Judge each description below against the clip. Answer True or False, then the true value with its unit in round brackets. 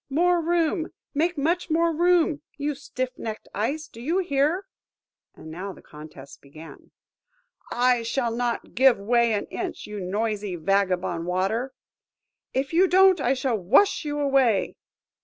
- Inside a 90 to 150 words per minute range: True (140 wpm)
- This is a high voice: True (260 Hz)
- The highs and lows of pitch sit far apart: True (7.8 semitones)